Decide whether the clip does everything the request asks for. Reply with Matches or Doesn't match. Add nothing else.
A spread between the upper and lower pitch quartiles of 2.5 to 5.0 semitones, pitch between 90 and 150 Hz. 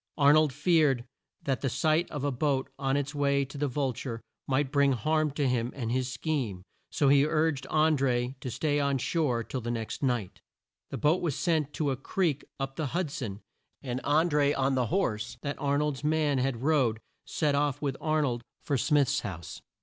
Matches